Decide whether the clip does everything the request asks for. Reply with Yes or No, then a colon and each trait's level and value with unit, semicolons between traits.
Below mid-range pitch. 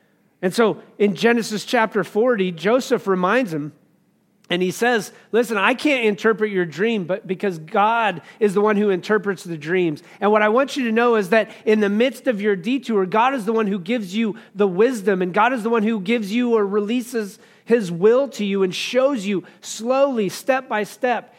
No: high, 215 Hz